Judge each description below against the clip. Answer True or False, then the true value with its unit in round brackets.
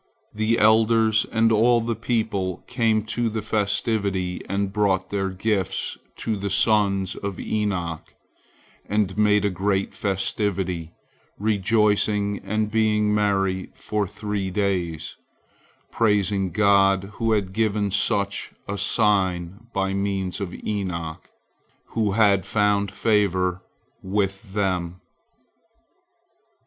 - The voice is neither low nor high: False (100 Hz)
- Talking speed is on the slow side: True (110 wpm)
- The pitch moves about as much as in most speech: False (1.9 semitones)